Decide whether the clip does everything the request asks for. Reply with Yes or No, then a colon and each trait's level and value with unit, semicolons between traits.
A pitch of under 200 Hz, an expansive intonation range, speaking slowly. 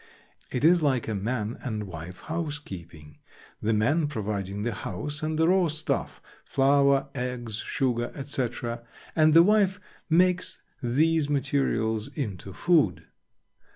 Yes: low, 135 Hz; wide, 6.2 semitones; slow, 120 wpm